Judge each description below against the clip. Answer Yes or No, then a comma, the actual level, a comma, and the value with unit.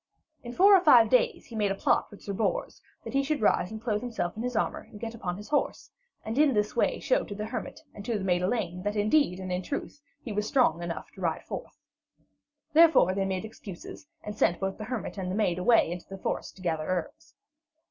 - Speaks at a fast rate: Yes, fast, 240 wpm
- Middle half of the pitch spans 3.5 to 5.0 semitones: Yes, average, 4.6 semitones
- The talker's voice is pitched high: Yes, high, 210 Hz